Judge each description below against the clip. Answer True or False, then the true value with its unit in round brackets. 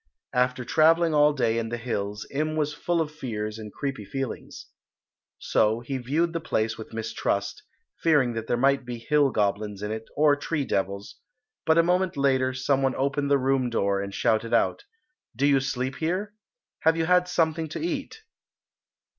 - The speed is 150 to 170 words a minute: False (180 wpm)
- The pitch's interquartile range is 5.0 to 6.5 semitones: True (5.6 semitones)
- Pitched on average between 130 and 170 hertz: True (135 Hz)